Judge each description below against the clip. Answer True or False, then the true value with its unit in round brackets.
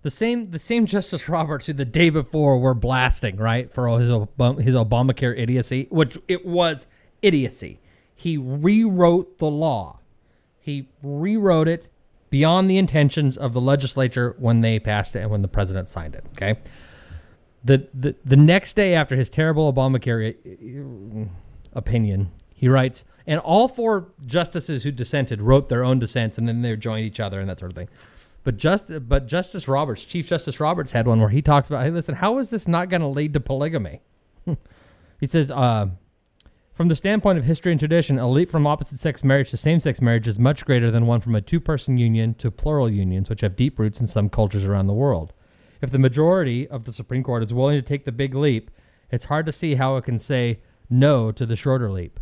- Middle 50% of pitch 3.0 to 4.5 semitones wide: False (5.3 semitones)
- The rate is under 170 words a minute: False (200 wpm)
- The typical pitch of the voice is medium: False (130 Hz)